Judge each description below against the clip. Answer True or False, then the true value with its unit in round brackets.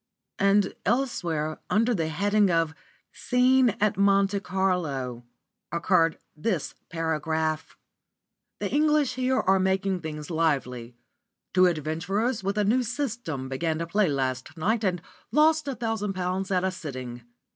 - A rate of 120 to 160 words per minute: True (135 wpm)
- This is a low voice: False (185 Hz)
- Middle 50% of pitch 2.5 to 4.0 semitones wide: False (5.1 semitones)